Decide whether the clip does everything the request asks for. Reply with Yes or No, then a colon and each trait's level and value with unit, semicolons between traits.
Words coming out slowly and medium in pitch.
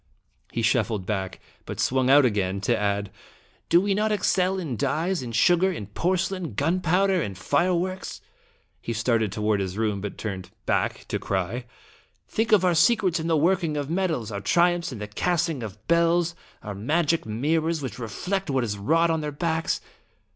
No: average, 180 wpm; medium, 150 Hz